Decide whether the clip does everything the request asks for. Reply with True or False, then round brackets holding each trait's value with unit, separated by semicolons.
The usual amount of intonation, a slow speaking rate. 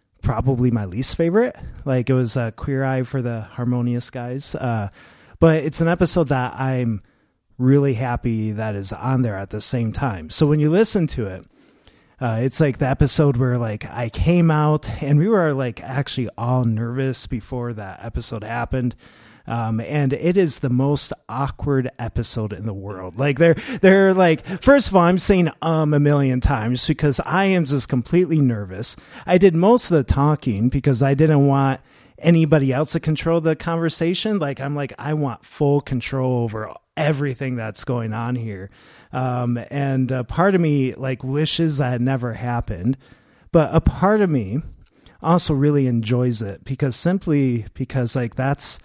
False (4.4 semitones; 175 wpm)